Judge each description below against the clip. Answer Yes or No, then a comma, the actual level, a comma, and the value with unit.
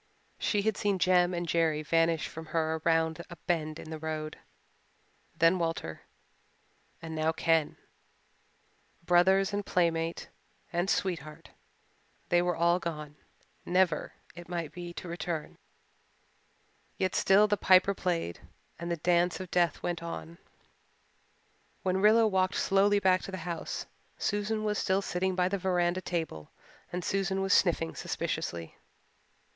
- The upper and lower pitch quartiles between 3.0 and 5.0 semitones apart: No, narrow, 2.5 semitones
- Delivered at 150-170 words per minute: No, average, 140 wpm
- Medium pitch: Yes, medium, 175 Hz